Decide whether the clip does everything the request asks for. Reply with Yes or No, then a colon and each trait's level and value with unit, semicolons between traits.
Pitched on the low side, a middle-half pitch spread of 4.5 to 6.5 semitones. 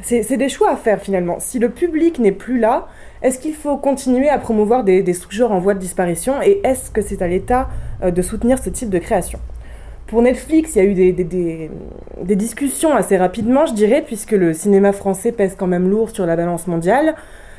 No: high, 210 Hz; wide, 5.6 semitones